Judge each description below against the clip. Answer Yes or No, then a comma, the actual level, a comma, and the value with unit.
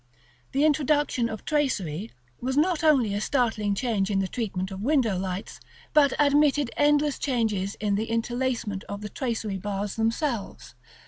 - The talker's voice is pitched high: Yes, high, 230 Hz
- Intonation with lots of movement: Yes, wide, 5.8 semitones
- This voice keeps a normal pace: Yes, average, 150 wpm